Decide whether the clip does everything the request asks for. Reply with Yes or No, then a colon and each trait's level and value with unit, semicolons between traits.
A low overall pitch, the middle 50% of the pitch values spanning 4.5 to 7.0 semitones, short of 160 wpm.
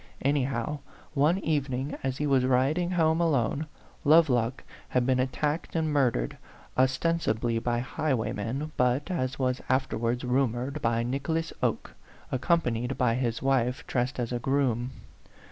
No: low, 130 Hz; average, 3.4 semitones; average, 150 wpm